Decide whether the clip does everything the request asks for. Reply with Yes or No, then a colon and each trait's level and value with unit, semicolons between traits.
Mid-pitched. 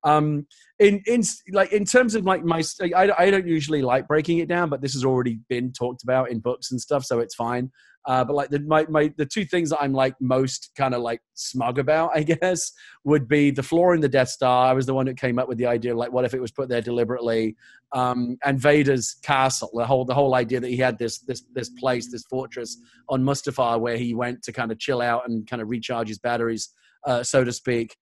No: low, 130 Hz